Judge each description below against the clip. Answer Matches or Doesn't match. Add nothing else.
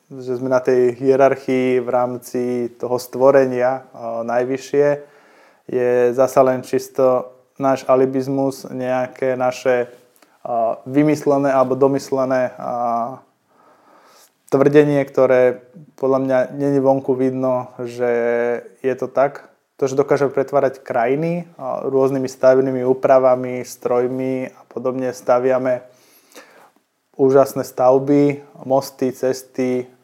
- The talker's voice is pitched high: Doesn't match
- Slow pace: Matches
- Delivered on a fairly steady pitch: Matches